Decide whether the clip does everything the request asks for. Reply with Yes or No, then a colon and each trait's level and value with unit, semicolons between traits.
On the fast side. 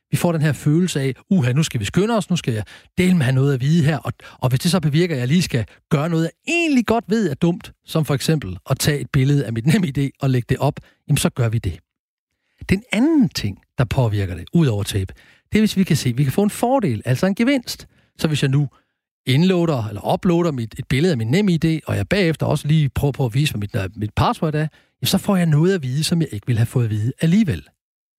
Yes: fast, 270 wpm